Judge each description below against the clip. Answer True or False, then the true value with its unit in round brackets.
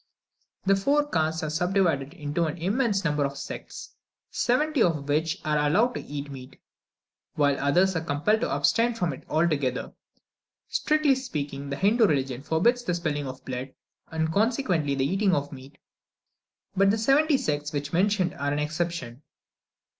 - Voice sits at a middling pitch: True (160 Hz)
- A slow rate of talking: False (160 wpm)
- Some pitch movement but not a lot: False (5.8 semitones)